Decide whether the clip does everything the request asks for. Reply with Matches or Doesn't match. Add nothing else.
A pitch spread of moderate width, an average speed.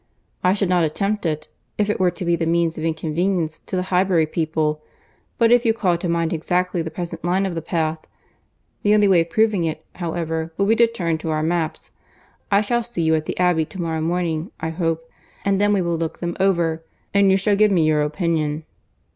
Doesn't match